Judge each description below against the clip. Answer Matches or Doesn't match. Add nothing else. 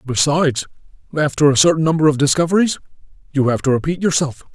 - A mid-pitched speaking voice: Matches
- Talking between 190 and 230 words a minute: Doesn't match